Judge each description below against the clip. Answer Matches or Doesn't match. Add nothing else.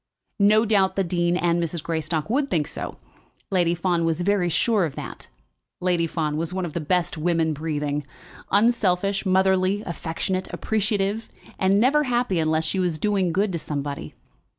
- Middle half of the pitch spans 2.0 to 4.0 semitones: Matches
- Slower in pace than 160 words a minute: Doesn't match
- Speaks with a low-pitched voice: Doesn't match